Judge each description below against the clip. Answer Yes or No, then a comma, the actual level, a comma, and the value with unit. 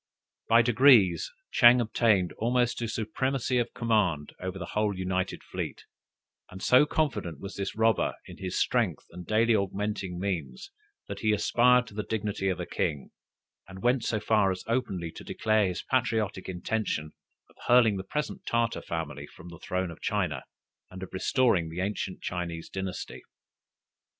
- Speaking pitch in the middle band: No, low, 100 Hz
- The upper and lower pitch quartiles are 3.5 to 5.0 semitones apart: Yes, average, 4.0 semitones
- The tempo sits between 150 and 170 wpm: Yes, average, 160 wpm